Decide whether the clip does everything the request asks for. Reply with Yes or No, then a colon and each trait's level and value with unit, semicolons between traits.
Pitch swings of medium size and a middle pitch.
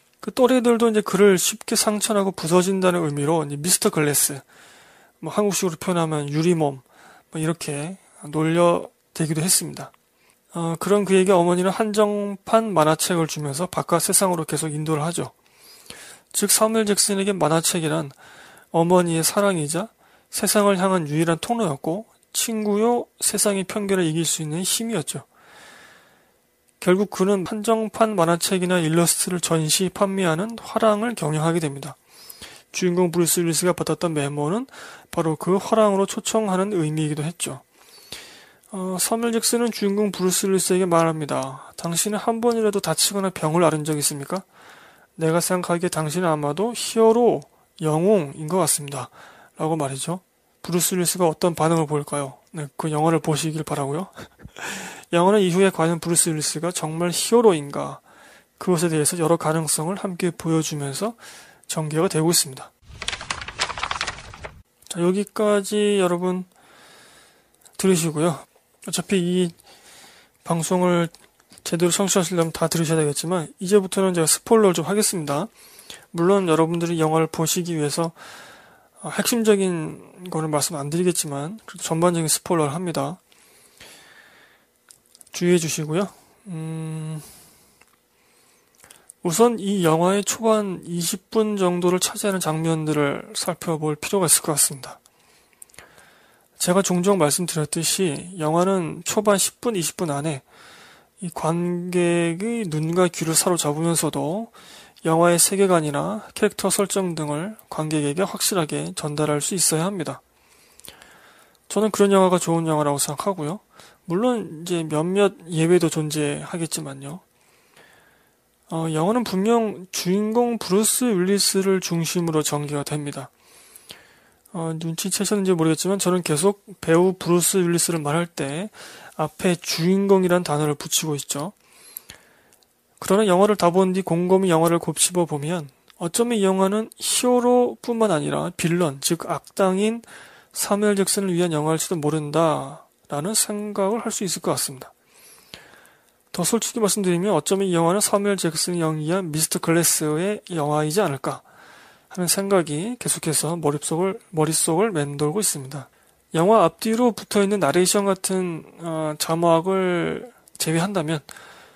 Yes: average, 3.8 semitones; medium, 175 Hz